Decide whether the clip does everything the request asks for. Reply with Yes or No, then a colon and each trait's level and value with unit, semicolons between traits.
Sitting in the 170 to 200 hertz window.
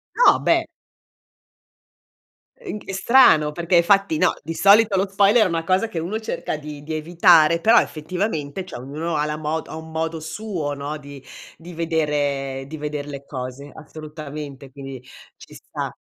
No: medium, 160 Hz